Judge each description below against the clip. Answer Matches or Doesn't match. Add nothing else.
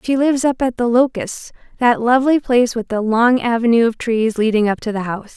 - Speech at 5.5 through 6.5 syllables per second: Matches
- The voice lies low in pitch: Doesn't match